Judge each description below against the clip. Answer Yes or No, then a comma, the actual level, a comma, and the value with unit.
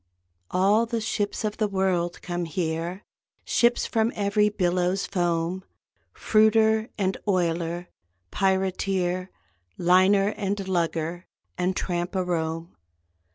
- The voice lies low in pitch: No, medium, 185 Hz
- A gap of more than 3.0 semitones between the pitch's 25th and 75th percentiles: No, average, 2.7 semitones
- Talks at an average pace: No, slow, 110 wpm